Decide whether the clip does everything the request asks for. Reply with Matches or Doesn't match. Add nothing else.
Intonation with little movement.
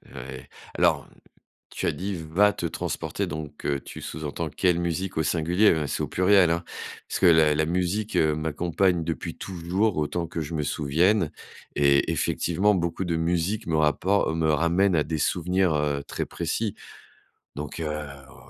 Doesn't match